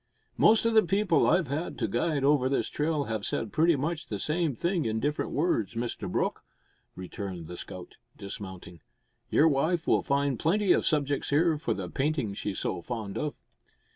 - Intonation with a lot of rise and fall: Yes, wide, 6.8 semitones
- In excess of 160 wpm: Yes, average, 180 wpm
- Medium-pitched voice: Yes, medium, 145 Hz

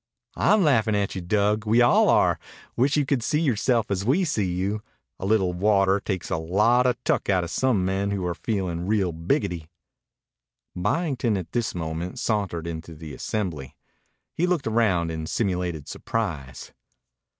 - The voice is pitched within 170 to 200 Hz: No, low, 100 Hz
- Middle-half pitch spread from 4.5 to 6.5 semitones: Yes, average, 4.8 semitones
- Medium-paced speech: Yes, average, 160 wpm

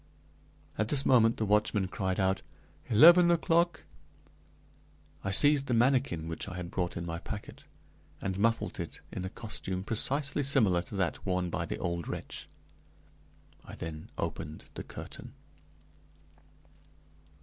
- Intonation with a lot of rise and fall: Yes, wide, 6.7 semitones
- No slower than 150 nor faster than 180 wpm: No, average, 140 wpm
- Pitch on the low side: Yes, low, 100 Hz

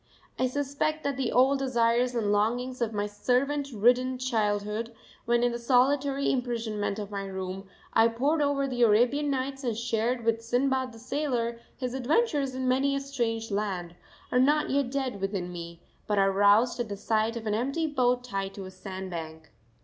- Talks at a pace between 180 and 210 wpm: Yes, average, 185 wpm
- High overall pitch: Yes, high, 240 Hz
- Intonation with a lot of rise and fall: No, average, 4.1 semitones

